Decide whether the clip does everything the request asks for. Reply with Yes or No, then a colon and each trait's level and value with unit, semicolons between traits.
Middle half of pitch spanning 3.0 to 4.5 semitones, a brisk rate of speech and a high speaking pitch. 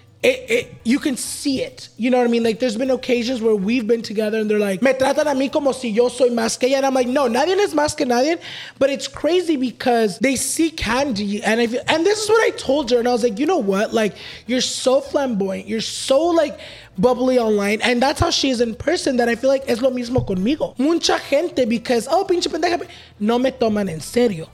Yes: average, 3.9 semitones; fast, 245 wpm; very high, 255 Hz